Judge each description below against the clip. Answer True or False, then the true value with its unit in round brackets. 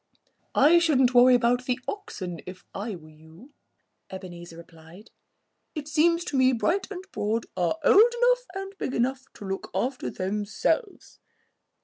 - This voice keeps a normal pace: True (150 wpm)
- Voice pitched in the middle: False (245 Hz)